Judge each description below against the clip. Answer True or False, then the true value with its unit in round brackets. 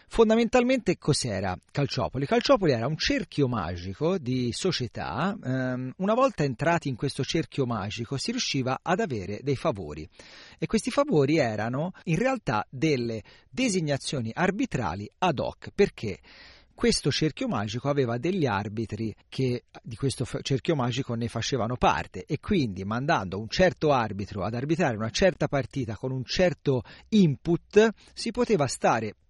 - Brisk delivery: False (135 wpm)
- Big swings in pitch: True (7.1 semitones)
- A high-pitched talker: False (140 Hz)